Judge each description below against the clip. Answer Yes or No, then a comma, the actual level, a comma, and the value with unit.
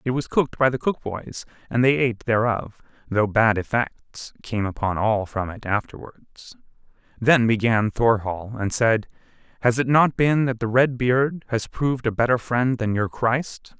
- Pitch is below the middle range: Yes, low, 120 Hz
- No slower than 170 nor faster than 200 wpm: Yes, average, 175 wpm